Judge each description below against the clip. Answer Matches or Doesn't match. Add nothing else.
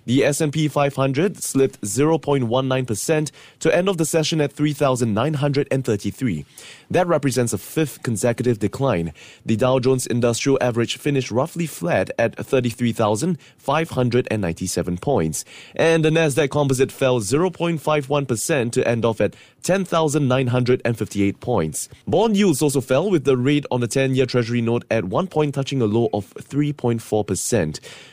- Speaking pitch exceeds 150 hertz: Doesn't match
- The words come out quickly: Doesn't match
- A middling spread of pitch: Matches